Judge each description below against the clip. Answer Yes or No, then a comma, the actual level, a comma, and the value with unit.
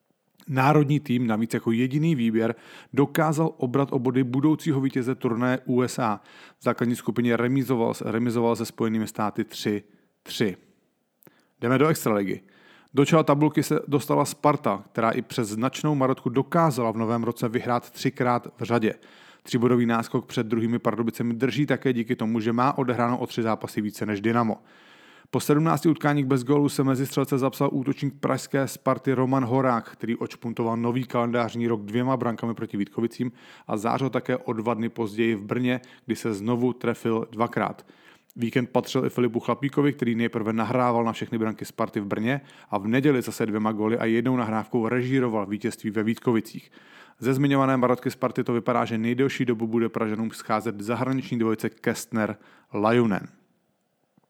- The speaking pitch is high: No, low, 120 Hz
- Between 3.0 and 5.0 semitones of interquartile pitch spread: No, narrow, 2.6 semitones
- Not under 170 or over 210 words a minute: No, average, 155 wpm